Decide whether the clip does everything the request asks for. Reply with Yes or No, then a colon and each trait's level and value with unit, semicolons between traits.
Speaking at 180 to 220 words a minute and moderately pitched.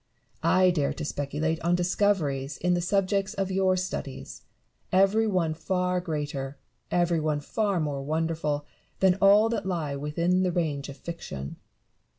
No: average, 150 wpm; medium, 170 Hz